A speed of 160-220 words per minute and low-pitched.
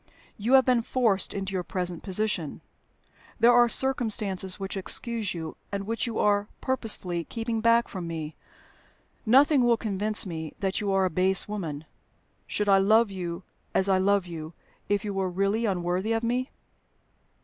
No: average, 165 wpm; high, 200 Hz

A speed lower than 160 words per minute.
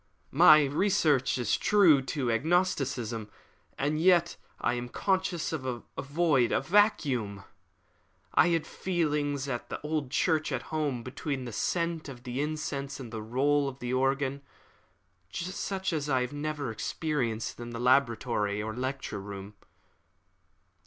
Yes: average, 145 wpm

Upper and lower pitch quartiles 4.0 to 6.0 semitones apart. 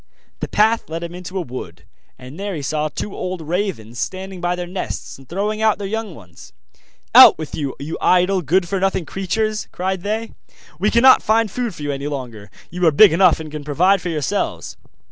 Yes: average, 4.8 semitones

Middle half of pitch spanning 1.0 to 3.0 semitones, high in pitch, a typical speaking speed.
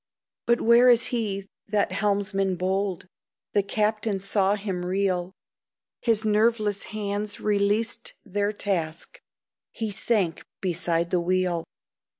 No: narrow, 2.4 semitones; high, 200 Hz; slow, 115 wpm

